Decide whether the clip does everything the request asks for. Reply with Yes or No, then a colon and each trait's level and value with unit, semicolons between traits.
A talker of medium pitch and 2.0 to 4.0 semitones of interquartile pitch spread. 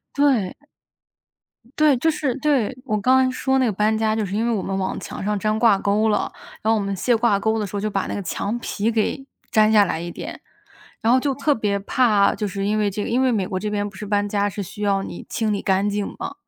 No: high, 210 Hz; average, 2.8 semitones